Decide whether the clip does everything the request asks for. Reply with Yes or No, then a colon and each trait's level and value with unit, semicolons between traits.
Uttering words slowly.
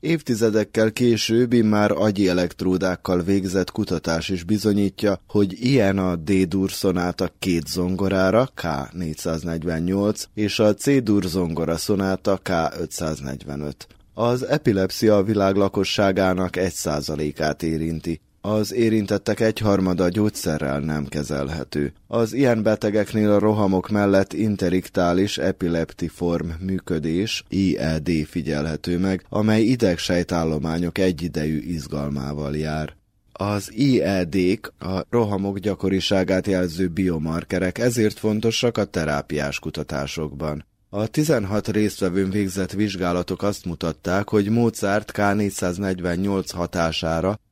Yes: slow, 95 wpm